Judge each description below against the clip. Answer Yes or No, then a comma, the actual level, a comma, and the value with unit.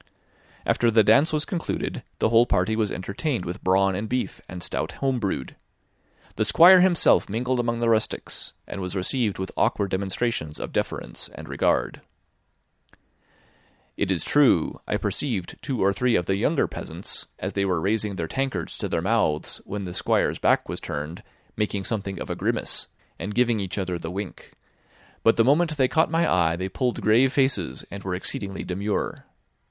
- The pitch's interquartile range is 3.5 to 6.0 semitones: Yes, average, 4.9 semitones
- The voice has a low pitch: Yes, low, 105 Hz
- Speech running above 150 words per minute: Yes, average, 180 wpm